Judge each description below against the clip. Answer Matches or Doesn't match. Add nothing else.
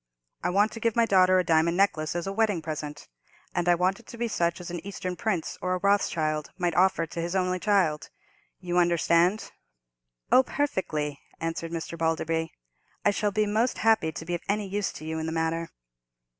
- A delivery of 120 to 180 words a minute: Doesn't match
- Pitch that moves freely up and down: Doesn't match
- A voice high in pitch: Doesn't match